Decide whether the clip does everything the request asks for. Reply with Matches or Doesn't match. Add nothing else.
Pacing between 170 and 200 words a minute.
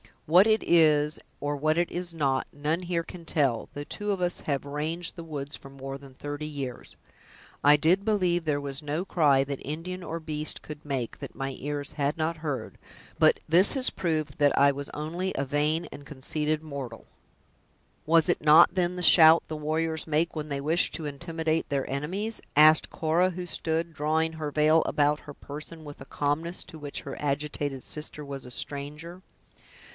Matches